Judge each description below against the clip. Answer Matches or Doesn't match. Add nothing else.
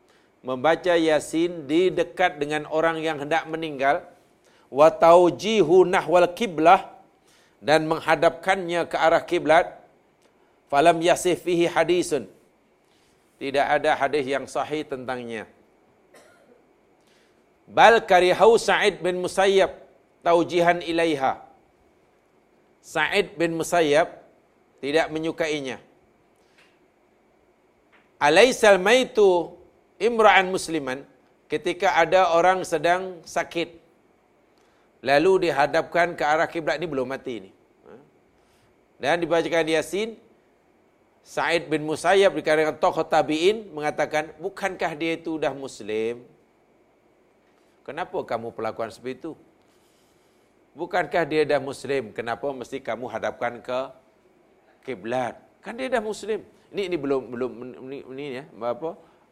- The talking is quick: Doesn't match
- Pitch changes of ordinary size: Matches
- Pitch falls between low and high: Matches